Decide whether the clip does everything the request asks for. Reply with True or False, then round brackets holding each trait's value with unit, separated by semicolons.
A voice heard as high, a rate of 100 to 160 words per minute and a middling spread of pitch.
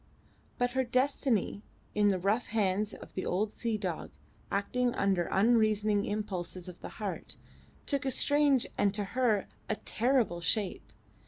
True (215 Hz; 150 wpm; 3.8 semitones)